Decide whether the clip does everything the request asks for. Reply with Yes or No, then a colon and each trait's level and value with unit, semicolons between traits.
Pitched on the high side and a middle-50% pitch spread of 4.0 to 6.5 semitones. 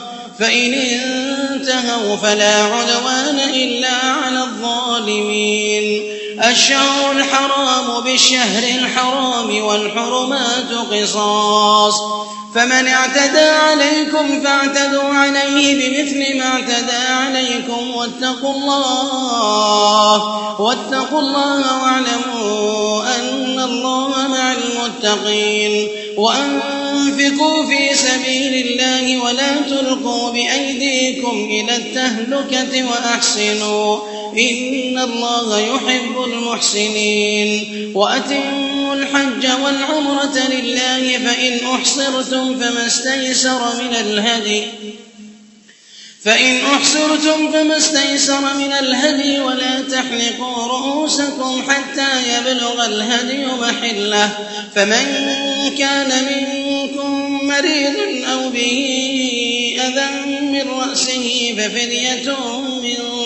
No: very high, 255 Hz; average, 2.7 semitones